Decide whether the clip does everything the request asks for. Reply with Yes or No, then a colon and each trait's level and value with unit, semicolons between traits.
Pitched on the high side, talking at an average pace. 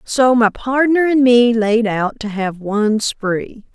Yes: high, 230 Hz; average, 175 wpm